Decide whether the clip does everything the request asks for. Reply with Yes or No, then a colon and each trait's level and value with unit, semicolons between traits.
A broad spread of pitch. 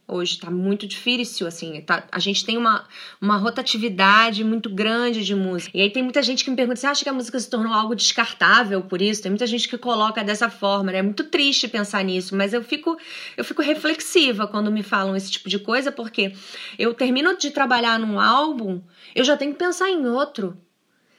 No: average, 4.5 semitones